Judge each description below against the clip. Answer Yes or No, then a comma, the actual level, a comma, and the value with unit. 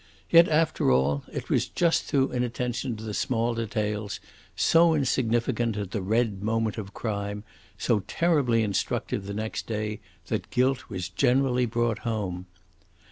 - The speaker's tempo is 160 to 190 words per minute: No, average, 145 wpm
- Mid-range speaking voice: No, low, 115 Hz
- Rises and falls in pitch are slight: No, average, 3.3 semitones